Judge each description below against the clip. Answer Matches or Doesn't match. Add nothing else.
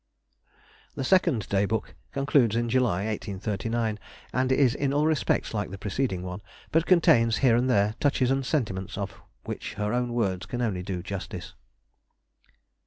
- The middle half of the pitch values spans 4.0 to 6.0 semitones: Matches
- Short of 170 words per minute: Matches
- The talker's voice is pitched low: Matches